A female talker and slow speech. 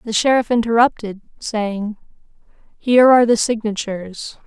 Yes: female; slow, 95 wpm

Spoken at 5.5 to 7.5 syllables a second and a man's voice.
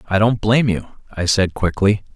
Yes: 5.6 syllables/s; male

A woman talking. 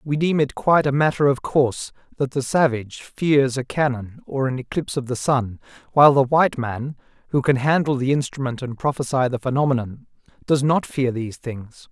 No: male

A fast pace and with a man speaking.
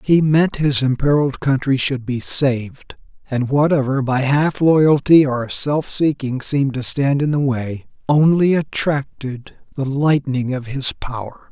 No: average, 150 wpm; male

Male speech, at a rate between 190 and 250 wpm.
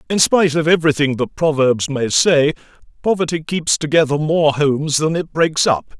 No: male; average, 170 wpm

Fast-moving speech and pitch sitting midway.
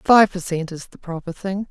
Yes: fast, 245 wpm; medium, 180 Hz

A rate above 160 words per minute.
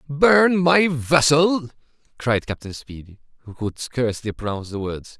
No: average, 140 wpm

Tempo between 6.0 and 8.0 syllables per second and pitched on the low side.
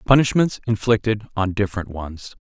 No: 5.2 syllables/s; low, 105 Hz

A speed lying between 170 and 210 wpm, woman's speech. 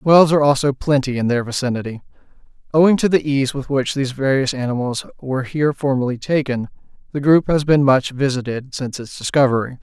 No: average, 175 wpm; male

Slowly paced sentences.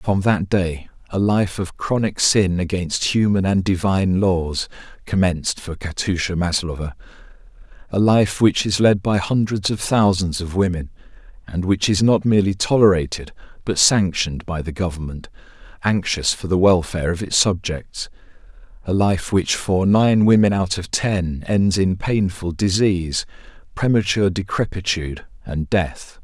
No: average, 145 wpm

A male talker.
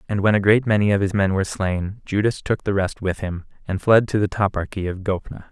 Yes: male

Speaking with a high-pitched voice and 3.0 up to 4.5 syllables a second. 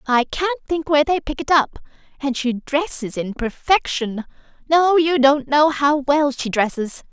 Yes: very high, 285 Hz; 4.4 syllables/s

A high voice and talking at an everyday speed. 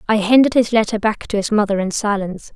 No: high, 210 Hz; fast, 235 wpm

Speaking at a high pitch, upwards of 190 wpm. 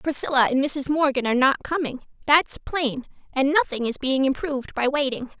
No: very high, 275 Hz; average, 180 wpm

